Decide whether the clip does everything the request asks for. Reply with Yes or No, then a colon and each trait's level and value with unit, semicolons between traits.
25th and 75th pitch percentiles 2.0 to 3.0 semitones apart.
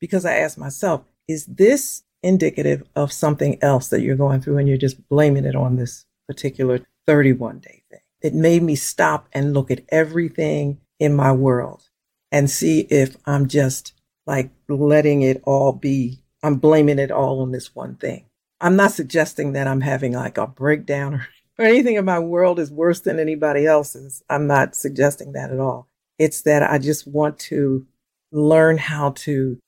Yes: narrow, 2.6 semitones